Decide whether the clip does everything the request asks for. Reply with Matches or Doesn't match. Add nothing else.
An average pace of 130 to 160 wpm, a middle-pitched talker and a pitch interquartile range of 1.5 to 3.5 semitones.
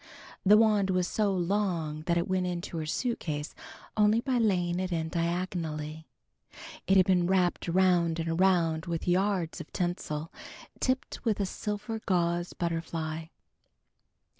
Matches